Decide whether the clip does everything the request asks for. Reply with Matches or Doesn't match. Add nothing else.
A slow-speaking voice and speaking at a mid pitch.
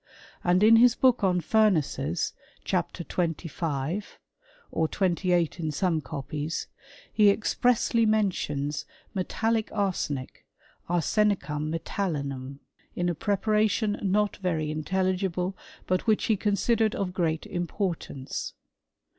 Matches